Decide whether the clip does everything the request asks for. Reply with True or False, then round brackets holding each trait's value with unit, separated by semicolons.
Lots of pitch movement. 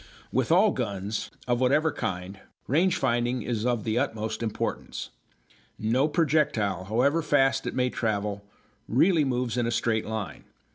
False (4.2 semitones)